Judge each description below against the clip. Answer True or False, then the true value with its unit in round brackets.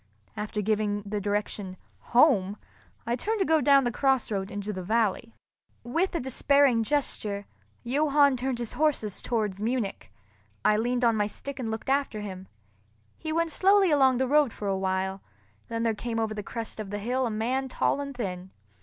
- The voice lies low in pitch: False (230 Hz)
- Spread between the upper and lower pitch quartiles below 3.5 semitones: False (4.6 semitones)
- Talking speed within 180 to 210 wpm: True (185 wpm)